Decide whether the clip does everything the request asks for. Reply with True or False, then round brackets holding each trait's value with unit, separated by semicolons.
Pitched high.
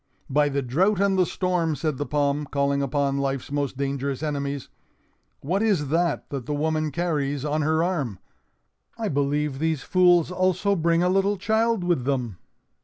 False (150 Hz)